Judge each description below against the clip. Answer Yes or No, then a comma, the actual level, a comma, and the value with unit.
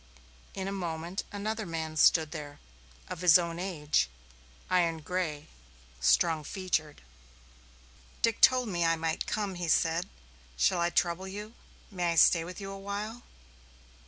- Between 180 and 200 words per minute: No, average, 140 wpm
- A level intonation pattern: No, average, 3.2 semitones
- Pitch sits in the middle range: Yes, medium, 175 Hz